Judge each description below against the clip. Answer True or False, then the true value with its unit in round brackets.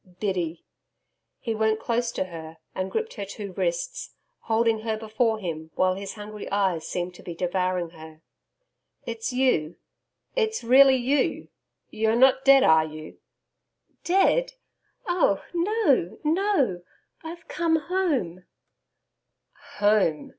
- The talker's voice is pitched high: True (220 Hz)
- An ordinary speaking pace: False (125 wpm)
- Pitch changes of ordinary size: False (7.3 semitones)